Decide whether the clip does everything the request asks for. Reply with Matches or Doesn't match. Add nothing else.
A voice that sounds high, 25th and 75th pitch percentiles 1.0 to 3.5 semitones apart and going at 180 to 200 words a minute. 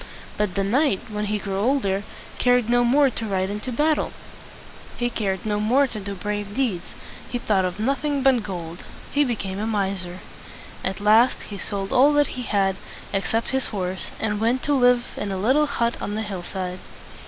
Doesn't match